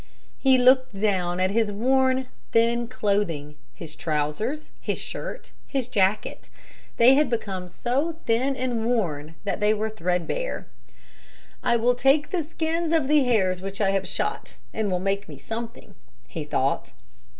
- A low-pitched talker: No, high, 225 Hz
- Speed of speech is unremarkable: Yes, average, 150 wpm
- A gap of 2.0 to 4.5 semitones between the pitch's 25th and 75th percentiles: No, wide, 5.5 semitones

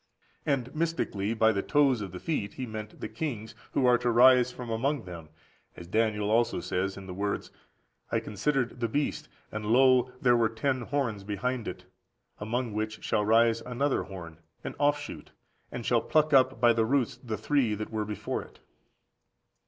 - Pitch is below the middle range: Yes, low, 115 Hz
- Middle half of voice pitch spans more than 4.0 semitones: No, average, 3.6 semitones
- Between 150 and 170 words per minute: No, average, 180 wpm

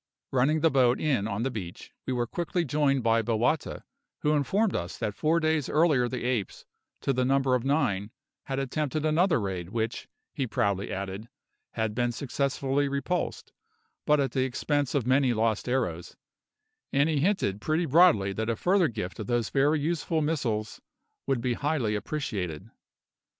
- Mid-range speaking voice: No, low, 130 Hz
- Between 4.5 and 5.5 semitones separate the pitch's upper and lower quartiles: Yes, average, 5.2 semitones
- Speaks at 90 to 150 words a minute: No, average, 165 wpm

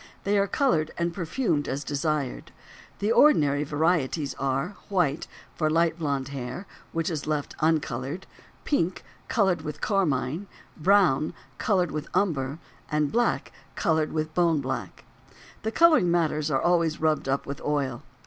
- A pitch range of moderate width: Yes, average, 3.8 semitones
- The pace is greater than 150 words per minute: No, average, 140 wpm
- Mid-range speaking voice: Yes, medium, 155 Hz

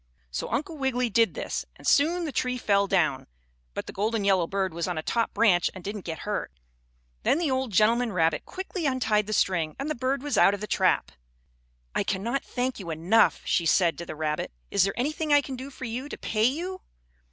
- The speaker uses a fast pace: Yes, fast, 220 wpm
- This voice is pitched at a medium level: No, high, 225 Hz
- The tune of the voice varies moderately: No, wide, 5.9 semitones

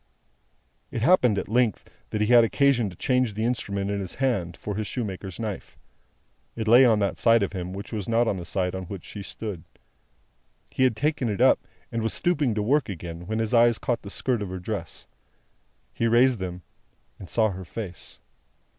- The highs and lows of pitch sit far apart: No, average, 3.7 semitones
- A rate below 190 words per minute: No, average, 200 wpm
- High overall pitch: No, low, 110 Hz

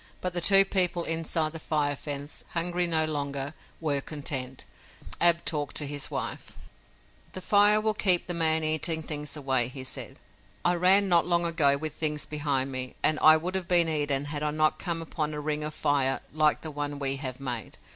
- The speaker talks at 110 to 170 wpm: No, average, 195 wpm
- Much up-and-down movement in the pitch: No, average, 2.9 semitones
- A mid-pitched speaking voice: Yes, medium, 155 Hz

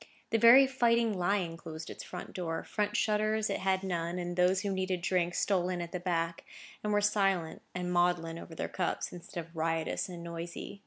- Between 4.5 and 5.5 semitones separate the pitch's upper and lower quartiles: No, average, 3.0 semitones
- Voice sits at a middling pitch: Yes, medium, 180 Hz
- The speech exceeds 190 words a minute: Yes, average, 200 wpm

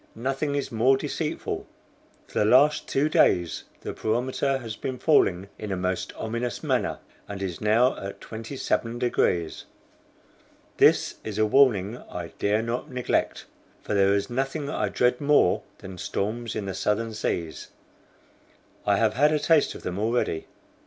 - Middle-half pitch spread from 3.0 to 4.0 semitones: No, average, 4.8 semitones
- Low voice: Yes, low, 115 Hz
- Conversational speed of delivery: Yes, average, 155 wpm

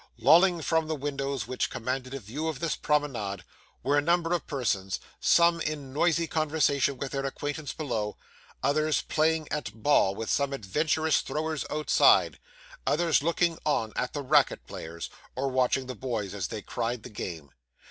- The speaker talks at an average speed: Yes, average, 165 wpm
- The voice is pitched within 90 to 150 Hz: Yes, medium, 140 Hz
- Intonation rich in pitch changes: No, average, 4.0 semitones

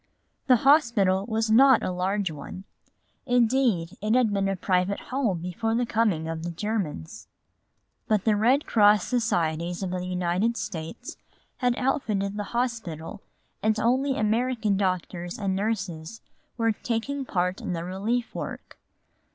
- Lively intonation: No, average, 4.3 semitones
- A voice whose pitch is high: Yes, high, 210 Hz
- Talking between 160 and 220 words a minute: No, average, 145 wpm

